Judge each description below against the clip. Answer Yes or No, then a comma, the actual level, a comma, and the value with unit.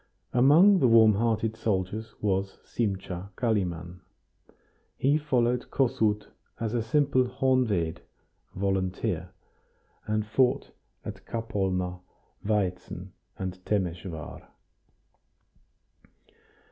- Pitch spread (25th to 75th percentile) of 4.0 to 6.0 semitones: Yes, average, 4.6 semitones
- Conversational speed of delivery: No, slow, 85 wpm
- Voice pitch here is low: Yes, low, 105 Hz